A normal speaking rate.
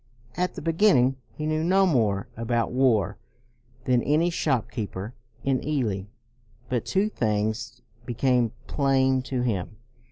No: slow, 130 wpm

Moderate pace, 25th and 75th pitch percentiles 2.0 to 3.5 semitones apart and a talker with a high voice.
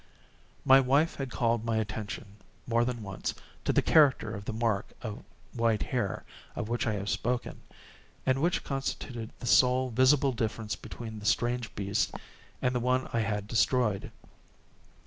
No: average, 160 wpm; average, 2.8 semitones; low, 120 Hz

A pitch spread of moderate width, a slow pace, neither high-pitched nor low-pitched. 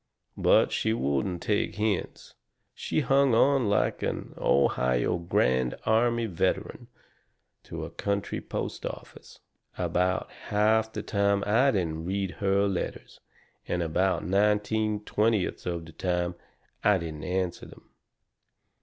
No: average, 3.8 semitones; slow, 125 wpm; low, 100 Hz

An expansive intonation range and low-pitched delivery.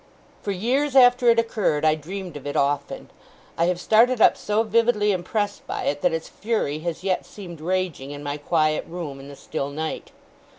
No: wide, 6.2 semitones; medium, 180 Hz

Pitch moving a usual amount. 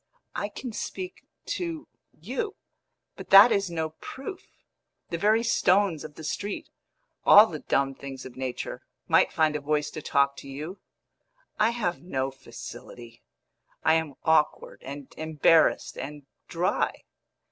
No: wide, 6.6 semitones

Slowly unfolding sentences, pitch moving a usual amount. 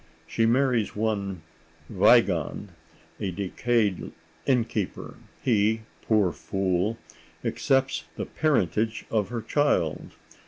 Yes: slow, 90 wpm; average, 3.5 semitones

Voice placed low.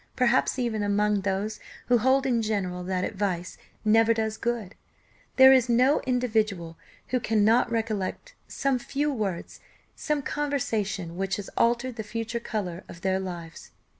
No: high, 220 Hz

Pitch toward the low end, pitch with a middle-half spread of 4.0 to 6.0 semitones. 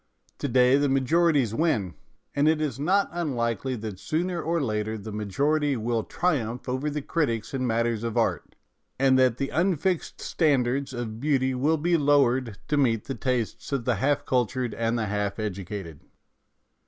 Yes: low, 130 Hz; average, 4.4 semitones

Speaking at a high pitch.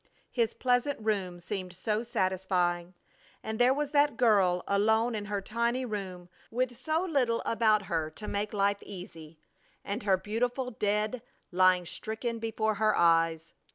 Yes: high, 210 Hz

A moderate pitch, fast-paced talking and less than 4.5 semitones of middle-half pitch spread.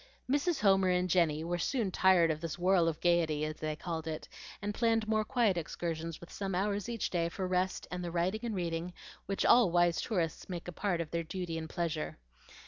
Yes: medium, 175 Hz; fast, 215 wpm; average, 2.9 semitones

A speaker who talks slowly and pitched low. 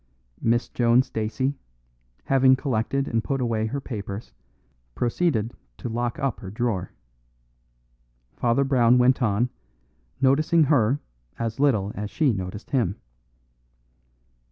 Yes: slow, 115 wpm; low, 120 Hz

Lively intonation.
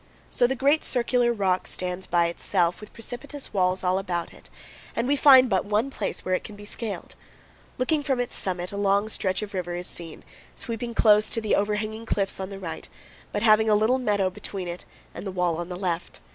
No: average, 4.1 semitones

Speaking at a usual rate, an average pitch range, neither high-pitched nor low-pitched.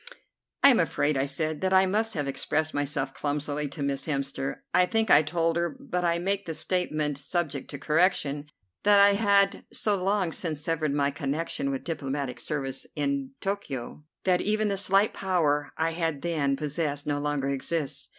Yes: average, 175 wpm; average, 4.5 semitones; medium, 155 Hz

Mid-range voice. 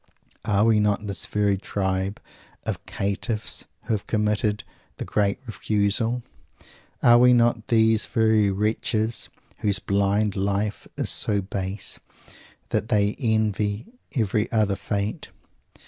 No: low, 105 Hz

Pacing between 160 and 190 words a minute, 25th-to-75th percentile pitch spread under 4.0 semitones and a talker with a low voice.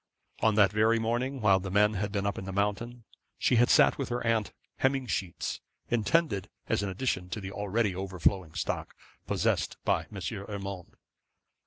Yes: average, 175 wpm; average, 3.2 semitones; low, 105 Hz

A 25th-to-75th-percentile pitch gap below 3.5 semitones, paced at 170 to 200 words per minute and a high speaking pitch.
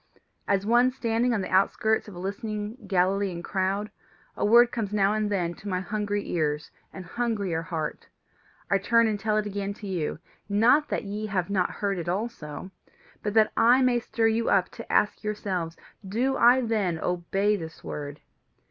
Yes: average, 3.1 semitones; average, 180 wpm; high, 205 Hz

